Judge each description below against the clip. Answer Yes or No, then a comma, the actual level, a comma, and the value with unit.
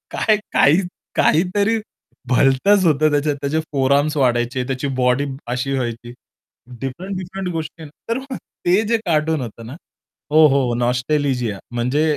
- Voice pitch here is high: No, medium, 145 Hz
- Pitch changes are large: No, average, 4.7 semitones